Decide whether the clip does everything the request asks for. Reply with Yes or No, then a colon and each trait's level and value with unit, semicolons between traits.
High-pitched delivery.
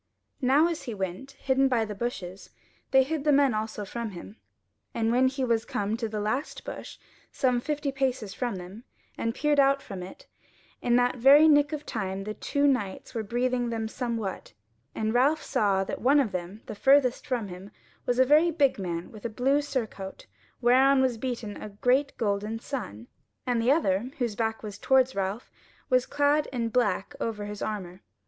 Yes: high, 240 Hz